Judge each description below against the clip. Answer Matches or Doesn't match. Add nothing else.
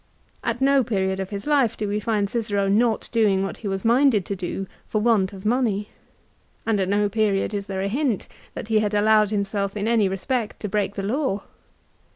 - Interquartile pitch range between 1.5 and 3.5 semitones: Matches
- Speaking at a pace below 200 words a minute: Doesn't match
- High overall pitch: Matches